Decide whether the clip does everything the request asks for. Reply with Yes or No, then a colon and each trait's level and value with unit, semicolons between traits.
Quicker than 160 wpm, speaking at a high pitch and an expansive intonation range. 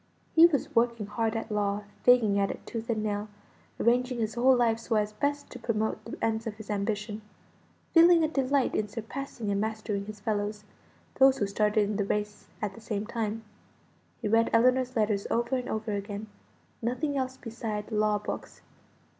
No: average, 180 wpm; high, 220 Hz; average, 2.8 semitones